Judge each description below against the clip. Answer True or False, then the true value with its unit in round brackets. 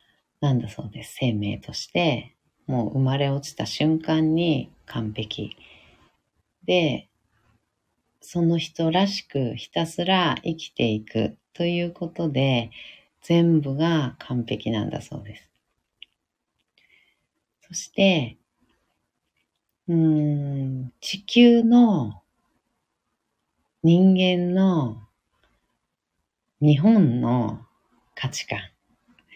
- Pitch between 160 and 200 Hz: False (140 Hz)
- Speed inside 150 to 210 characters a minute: True (155 characters per minute)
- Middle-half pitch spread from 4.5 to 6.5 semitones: False (7.0 semitones)